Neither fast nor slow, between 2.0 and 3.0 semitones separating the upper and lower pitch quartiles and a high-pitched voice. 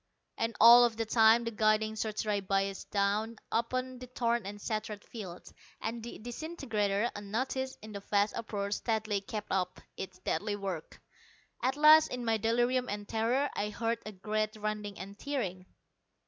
Yes: average, 160 wpm; narrow, 2.5 semitones; high, 215 Hz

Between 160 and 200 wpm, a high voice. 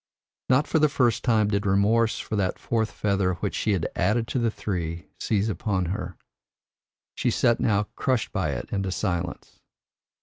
No: average, 170 wpm; low, 105 Hz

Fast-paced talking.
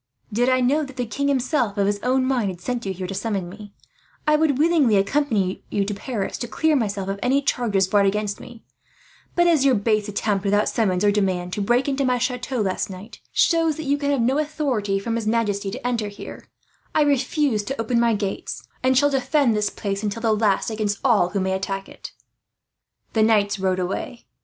Yes: fast, 215 wpm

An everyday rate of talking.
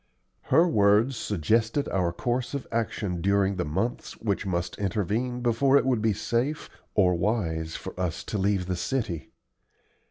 Yes: average, 155 wpm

